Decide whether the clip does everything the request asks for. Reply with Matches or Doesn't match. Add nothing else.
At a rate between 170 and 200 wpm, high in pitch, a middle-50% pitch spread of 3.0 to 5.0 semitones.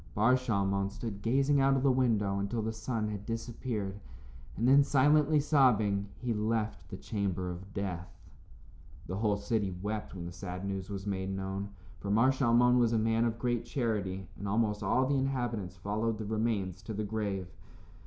Doesn't match